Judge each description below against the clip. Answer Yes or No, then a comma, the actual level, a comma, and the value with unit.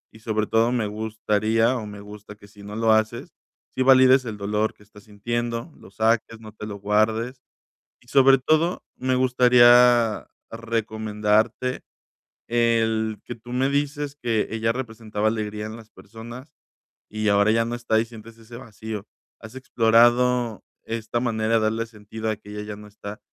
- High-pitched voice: No, low, 110 Hz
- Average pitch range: No, narrow, 2.1 semitones